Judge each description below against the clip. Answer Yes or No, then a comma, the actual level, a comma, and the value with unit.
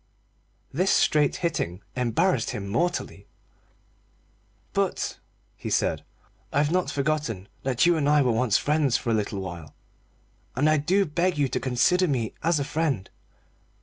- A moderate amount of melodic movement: No, wide, 5.9 semitones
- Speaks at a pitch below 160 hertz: Yes, medium, 140 Hz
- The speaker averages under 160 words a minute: Yes, average, 150 wpm